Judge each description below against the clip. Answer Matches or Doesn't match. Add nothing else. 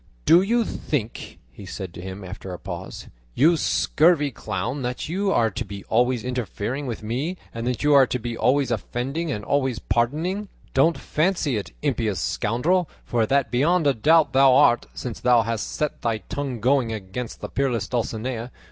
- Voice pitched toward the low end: Matches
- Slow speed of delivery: Doesn't match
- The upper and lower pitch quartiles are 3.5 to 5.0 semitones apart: Matches